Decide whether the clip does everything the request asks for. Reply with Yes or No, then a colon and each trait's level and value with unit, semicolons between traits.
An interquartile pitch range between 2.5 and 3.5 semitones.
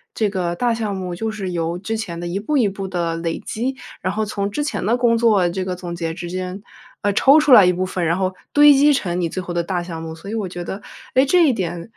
No: average, 4.2 semitones